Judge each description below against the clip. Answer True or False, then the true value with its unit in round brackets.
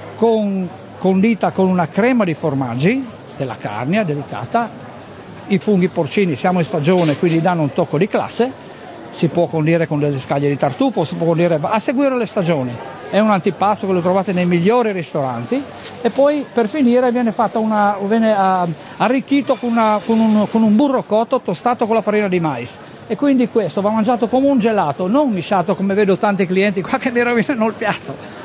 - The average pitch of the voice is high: True (200 Hz)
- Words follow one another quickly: True (185 wpm)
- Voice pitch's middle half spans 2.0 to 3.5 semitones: False (5.0 semitones)